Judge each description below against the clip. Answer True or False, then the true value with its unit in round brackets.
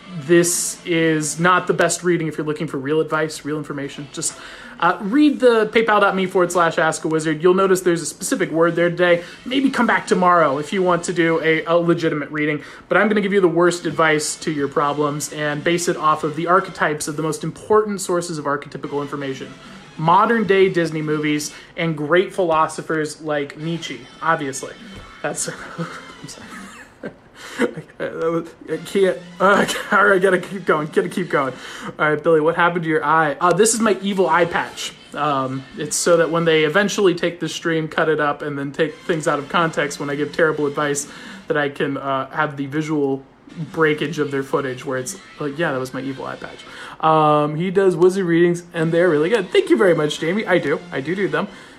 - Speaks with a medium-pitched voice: True (165 Hz)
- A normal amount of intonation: True (3.2 semitones)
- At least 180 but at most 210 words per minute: True (205 wpm)